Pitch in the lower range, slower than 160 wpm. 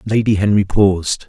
Yes: low, 100 Hz; average, 140 wpm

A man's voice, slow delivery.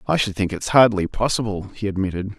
No: male; average, 200 wpm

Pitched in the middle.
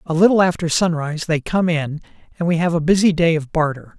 Yes: medium, 165 Hz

